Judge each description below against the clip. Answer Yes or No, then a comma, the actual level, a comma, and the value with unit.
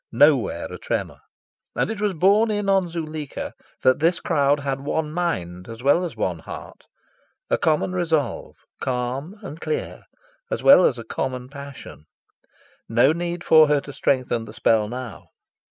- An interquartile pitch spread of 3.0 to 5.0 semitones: No, wide, 5.6 semitones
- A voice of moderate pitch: Yes, medium, 145 Hz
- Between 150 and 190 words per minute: Yes, average, 160 wpm